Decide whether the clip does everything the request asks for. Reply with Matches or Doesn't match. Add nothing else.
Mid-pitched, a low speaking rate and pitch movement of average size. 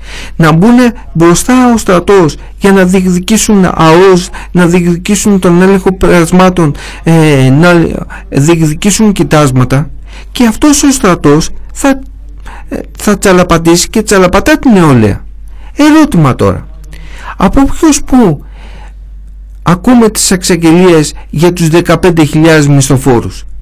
Matches